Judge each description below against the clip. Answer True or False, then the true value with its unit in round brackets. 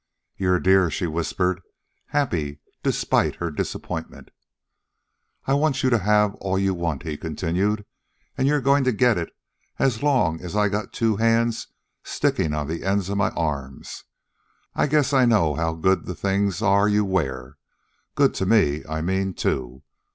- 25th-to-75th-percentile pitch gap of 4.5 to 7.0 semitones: True (5.2 semitones)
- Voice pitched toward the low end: True (95 Hz)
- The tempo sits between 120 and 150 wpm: False (165 wpm)